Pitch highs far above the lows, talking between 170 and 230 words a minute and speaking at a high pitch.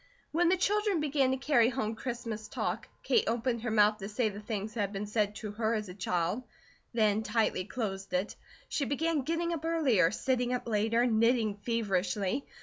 No: average, 4.0 semitones; average, 190 wpm; high, 225 Hz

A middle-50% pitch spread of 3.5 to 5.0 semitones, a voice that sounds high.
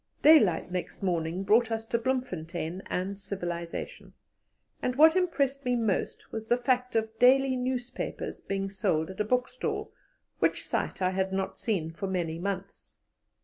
No: wide, 5.4 semitones; high, 205 Hz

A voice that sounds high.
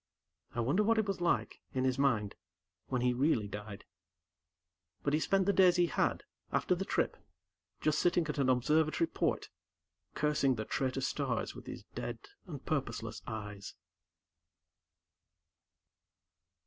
No: medium, 140 Hz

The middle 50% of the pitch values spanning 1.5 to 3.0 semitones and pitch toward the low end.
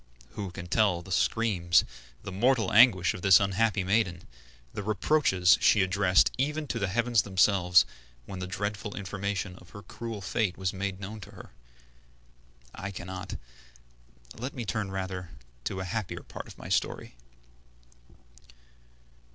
Yes: average, 2.7 semitones; low, 100 Hz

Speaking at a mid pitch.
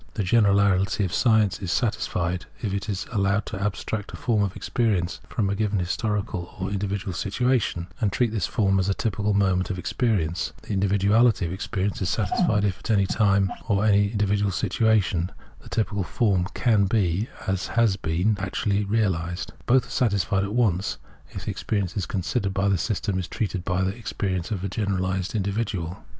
No: low, 100 Hz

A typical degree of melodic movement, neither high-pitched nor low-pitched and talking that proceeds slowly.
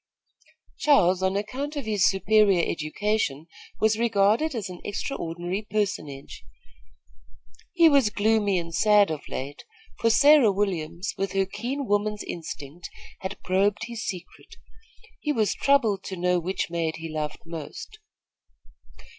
No: average, 4.1 semitones; high, 200 Hz; slow, 130 wpm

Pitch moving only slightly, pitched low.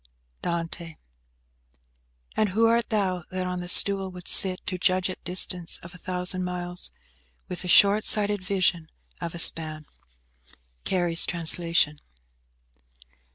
No: narrow, 1.8 semitones; medium, 180 Hz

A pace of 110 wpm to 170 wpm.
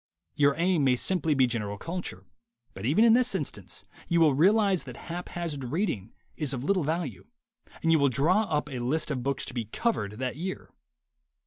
No: average, 190 wpm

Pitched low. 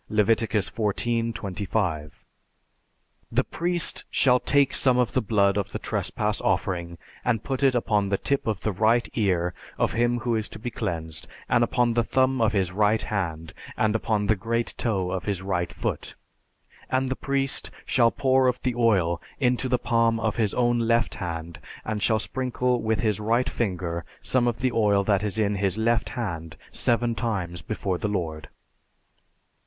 Yes: low, 110 Hz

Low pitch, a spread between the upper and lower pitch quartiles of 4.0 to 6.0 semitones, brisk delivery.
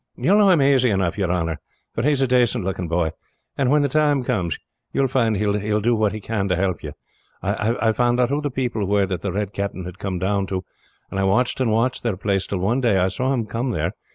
Yes: low, 105 Hz; average, 4.7 semitones; fast, 265 wpm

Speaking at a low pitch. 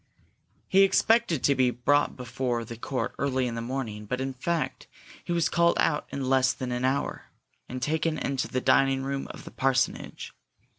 Yes: low, 130 Hz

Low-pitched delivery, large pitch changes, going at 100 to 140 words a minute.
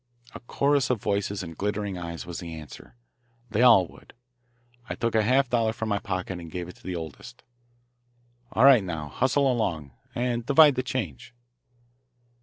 No: low, 105 Hz; wide, 6.2 semitones; average, 175 wpm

